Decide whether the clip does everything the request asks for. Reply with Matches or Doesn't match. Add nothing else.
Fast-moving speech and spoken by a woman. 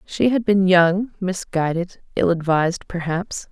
Doesn't match